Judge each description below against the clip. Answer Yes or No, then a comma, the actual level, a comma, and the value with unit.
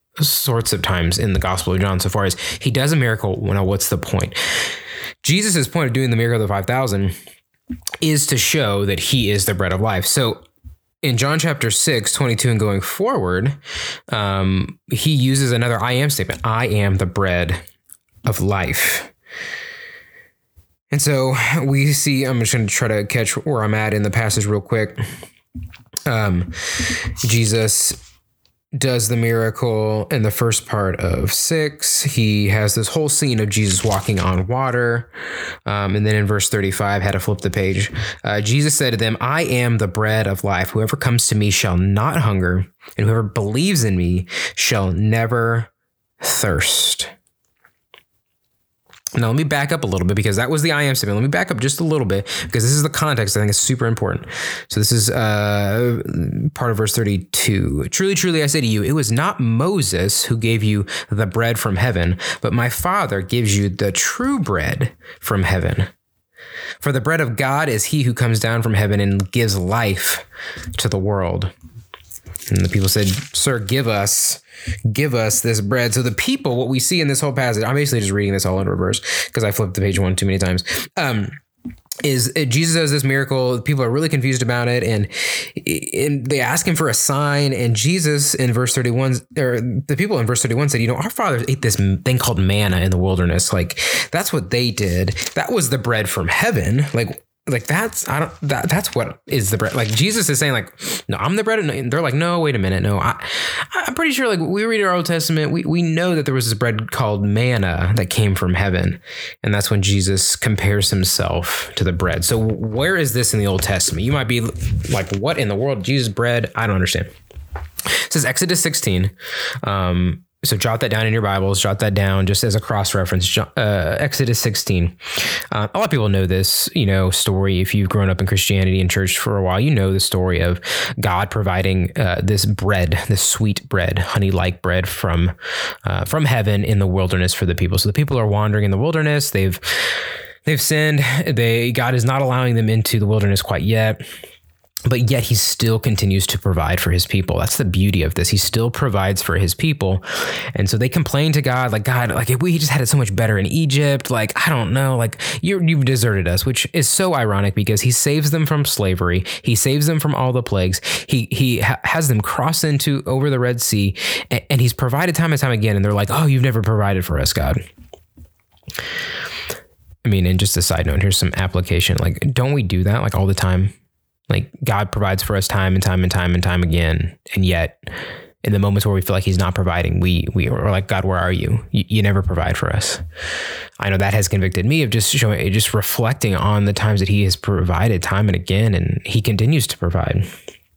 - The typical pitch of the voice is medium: No, low, 110 Hz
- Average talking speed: No, fast, 210 wpm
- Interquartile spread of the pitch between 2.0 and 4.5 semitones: No, wide, 5.4 semitones